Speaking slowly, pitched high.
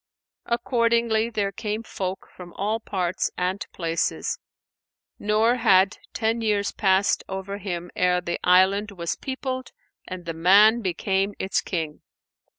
Yes: slow, 130 wpm; high, 200 Hz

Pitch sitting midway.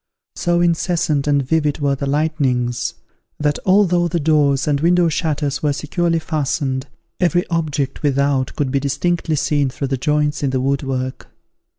Yes: medium, 150 Hz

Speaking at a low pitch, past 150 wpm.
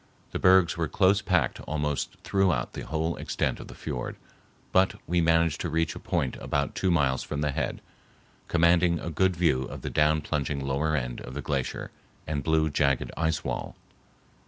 Yes: very low, 80 Hz; average, 180 wpm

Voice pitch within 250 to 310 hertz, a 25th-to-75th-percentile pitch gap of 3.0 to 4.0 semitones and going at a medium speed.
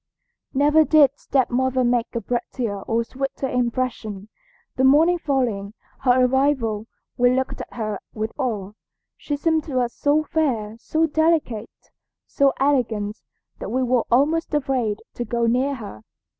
Yes: very high, 255 Hz; average, 3.7 semitones; average, 145 wpm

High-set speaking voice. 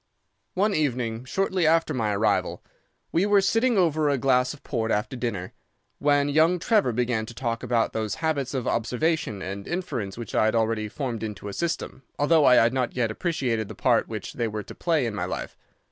No: low, 125 Hz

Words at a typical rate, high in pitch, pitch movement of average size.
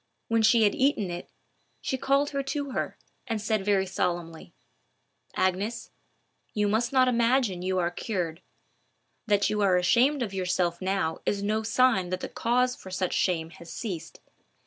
Yes: average, 165 wpm; high, 205 Hz; average, 4.7 semitones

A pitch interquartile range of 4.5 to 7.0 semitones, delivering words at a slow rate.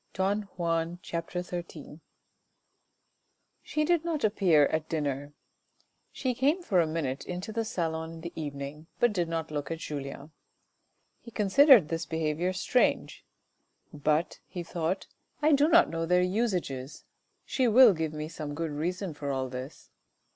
No: average, 4.8 semitones; average, 155 wpm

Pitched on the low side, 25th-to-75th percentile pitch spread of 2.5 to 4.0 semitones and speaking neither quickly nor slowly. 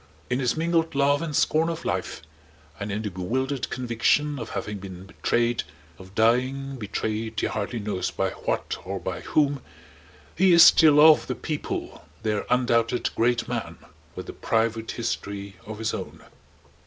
No: low, 120 Hz; average, 4.9 semitones; average, 160 wpm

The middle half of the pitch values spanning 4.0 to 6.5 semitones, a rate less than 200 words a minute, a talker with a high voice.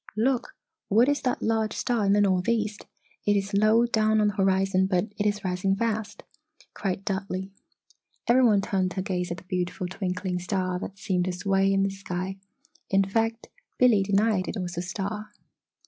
No: narrow, 2.5 semitones; average, 180 wpm; high, 195 Hz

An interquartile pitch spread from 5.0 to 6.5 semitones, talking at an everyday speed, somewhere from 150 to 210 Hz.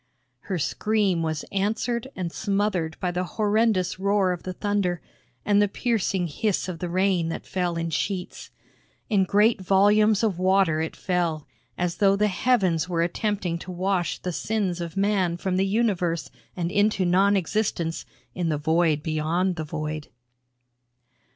No: average, 3.1 semitones; average, 155 wpm; medium, 185 Hz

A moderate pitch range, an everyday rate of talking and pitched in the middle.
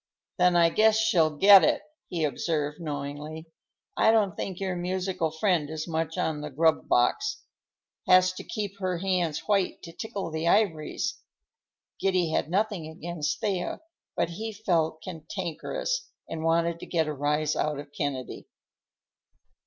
Yes: average, 3.4 semitones; average, 150 wpm; medium, 170 Hz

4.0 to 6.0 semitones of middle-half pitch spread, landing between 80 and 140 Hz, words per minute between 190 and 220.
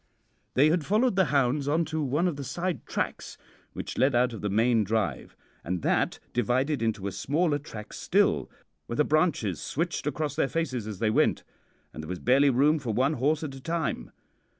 Yes: average, 5.1 semitones; low, 135 Hz; average, 195 wpm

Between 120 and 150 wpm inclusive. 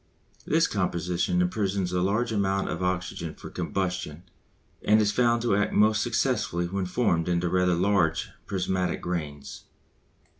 Yes: average, 140 wpm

